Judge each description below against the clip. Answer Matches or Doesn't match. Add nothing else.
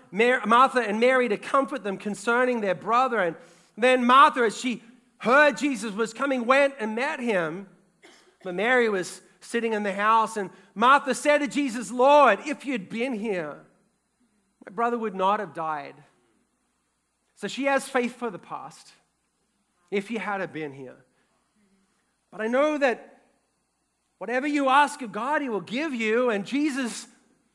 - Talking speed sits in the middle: Matches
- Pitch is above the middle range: Matches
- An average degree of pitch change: Matches